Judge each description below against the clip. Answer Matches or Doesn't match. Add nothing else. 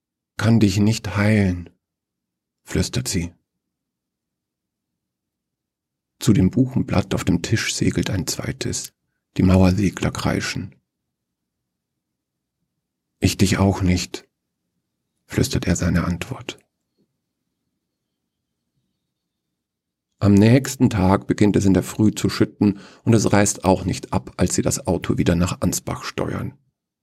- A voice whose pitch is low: Matches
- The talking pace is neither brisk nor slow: Doesn't match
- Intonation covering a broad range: Doesn't match